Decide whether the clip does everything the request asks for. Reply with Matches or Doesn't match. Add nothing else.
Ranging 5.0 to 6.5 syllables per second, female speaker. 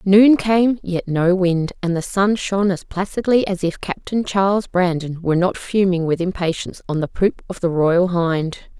Doesn't match